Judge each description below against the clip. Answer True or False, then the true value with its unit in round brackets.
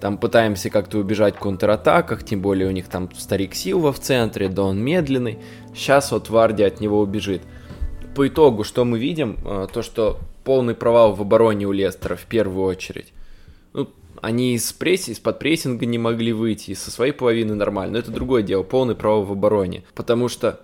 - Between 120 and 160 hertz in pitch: False (105 Hz)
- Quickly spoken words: True (185 wpm)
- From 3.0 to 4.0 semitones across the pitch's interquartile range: True (3.3 semitones)